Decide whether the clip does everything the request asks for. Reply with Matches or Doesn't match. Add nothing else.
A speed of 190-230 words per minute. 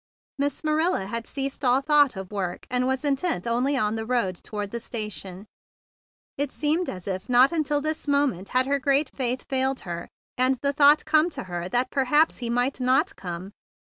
Matches